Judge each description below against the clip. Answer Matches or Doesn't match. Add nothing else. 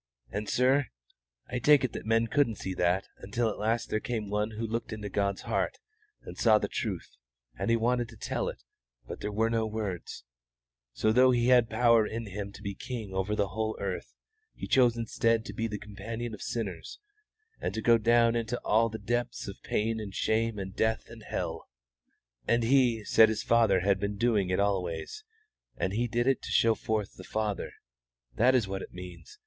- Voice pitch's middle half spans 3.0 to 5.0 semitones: Doesn't match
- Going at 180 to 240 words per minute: Matches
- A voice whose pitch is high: Doesn't match